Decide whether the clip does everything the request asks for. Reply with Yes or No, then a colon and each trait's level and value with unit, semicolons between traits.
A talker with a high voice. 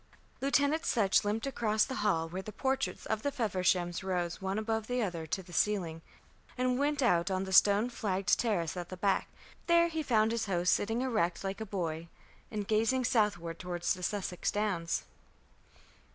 Yes: high, 205 Hz